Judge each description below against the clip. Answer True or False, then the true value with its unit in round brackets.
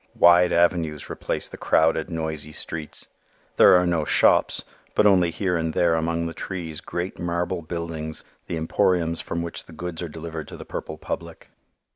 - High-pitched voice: False (85 Hz)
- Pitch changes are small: True (1.5 semitones)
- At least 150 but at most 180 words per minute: True (170 wpm)